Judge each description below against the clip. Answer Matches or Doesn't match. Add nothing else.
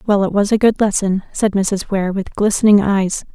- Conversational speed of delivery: Doesn't match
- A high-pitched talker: Matches